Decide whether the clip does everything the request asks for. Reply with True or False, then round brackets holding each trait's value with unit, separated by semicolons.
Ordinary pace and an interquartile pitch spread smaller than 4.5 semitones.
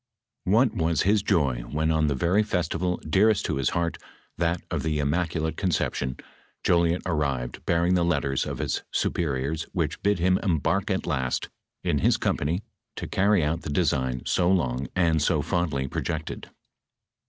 True (165 wpm; 3.7 semitones)